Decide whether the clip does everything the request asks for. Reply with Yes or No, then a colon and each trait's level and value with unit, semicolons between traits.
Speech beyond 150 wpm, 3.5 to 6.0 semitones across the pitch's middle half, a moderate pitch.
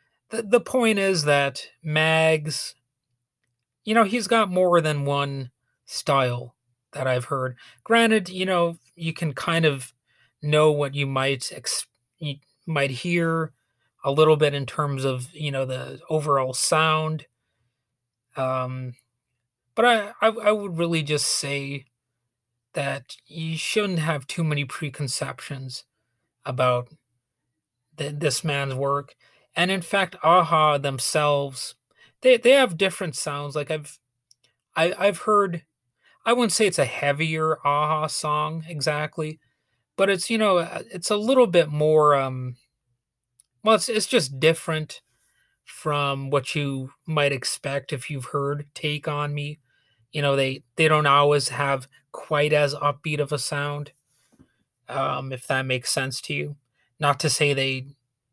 No: average, 140 wpm; average, 3.8 semitones; medium, 145 Hz